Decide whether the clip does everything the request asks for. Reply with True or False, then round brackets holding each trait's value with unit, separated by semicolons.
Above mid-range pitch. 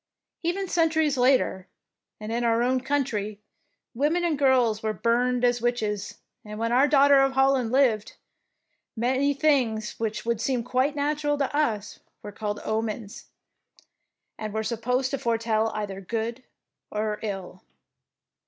True (240 Hz)